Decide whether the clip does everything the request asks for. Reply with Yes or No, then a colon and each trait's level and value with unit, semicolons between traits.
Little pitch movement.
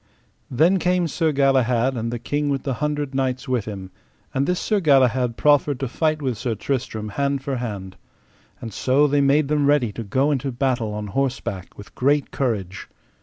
No: average, 3.6 semitones